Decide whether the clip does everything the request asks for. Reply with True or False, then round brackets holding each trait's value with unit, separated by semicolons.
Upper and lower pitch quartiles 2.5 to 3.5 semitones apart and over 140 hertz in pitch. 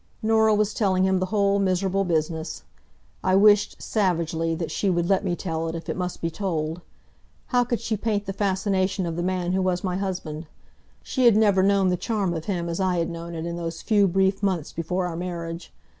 True (2.8 semitones; 185 Hz)